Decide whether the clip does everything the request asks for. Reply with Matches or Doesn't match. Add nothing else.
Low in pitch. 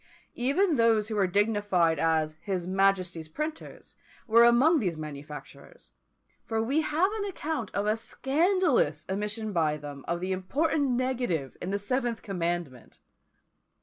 Doesn't match